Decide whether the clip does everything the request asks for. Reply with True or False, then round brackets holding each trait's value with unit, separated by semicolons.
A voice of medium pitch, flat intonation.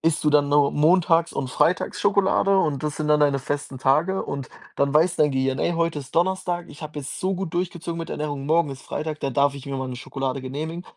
False (150 Hz; 3.4 semitones)